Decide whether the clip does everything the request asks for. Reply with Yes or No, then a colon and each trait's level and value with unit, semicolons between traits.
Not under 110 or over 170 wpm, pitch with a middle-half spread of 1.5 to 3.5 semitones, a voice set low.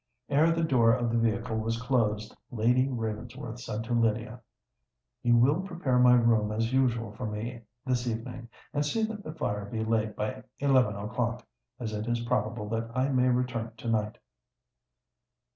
Yes: average, 160 wpm; narrow, 2.4 semitones; low, 120 Hz